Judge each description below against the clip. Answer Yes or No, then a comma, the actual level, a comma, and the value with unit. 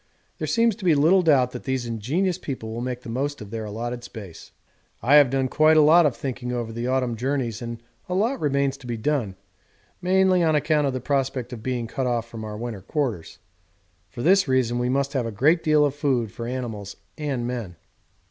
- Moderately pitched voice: No, low, 130 Hz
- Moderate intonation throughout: Yes, average, 4.0 semitones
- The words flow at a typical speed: No, fast, 215 wpm